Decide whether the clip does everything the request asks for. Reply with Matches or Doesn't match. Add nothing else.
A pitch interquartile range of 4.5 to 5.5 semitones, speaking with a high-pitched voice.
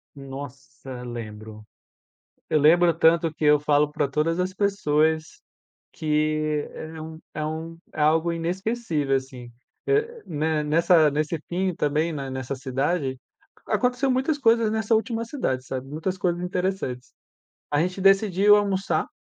Doesn't match